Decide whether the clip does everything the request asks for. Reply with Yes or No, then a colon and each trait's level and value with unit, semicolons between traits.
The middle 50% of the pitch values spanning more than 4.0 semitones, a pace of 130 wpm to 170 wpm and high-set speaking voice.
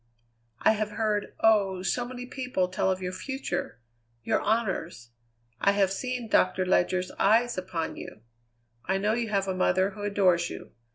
No: average, 3.3 semitones; average, 165 wpm; high, 195 Hz